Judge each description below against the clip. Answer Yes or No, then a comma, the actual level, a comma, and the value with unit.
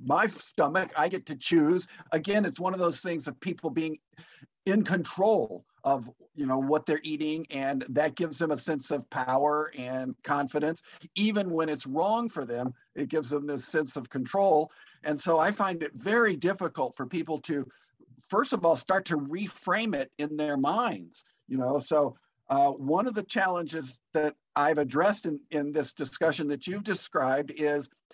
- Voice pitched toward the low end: No, medium, 155 Hz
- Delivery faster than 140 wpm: Yes, average, 180 wpm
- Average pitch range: Yes, average, 3.3 semitones